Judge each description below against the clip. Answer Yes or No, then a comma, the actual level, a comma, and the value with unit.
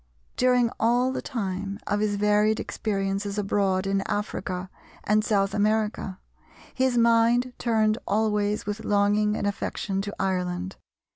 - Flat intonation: Yes, narrow, 1.9 semitones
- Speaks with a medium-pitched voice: No, high, 210 Hz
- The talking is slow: Yes, slow, 130 wpm